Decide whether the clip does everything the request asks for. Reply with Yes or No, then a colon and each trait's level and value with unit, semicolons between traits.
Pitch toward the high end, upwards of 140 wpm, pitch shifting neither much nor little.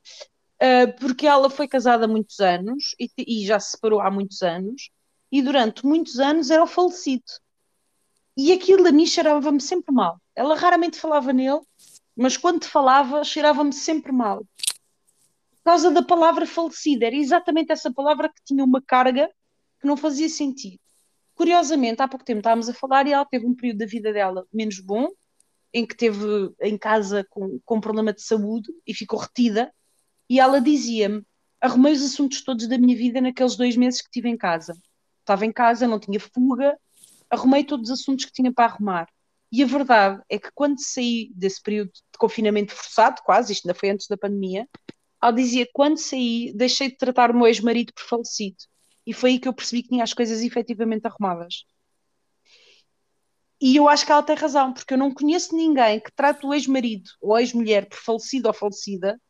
Yes: very high, 250 Hz; fast, 185 wpm; average, 4.7 semitones